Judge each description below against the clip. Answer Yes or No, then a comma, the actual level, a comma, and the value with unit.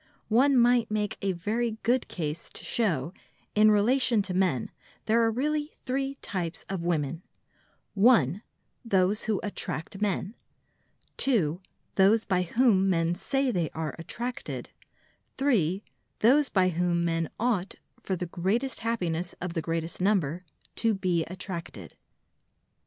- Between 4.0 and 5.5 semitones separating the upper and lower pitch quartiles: Yes, average, 5.2 semitones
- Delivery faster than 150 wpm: No, slow, 135 wpm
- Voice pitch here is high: Yes, high, 195 Hz